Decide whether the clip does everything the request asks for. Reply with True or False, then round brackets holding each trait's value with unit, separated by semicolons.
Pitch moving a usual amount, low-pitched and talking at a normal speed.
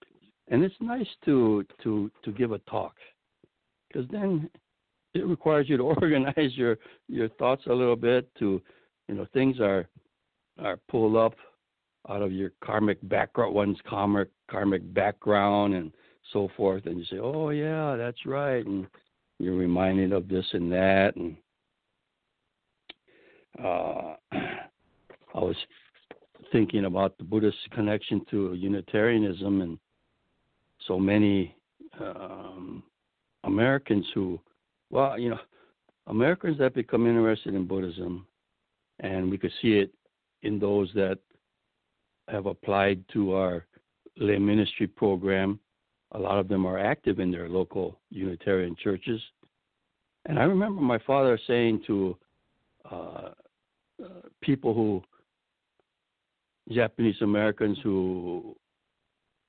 False (3.8 semitones; 105 Hz; 120 wpm)